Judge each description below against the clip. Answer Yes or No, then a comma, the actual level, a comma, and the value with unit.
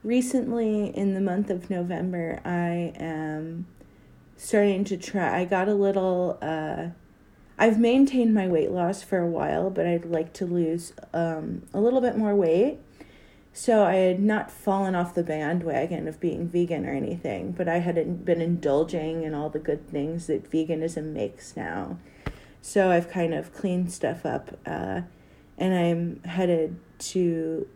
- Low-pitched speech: No, medium, 175 Hz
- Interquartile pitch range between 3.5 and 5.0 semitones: No, average, 3.0 semitones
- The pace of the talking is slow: No, average, 160 wpm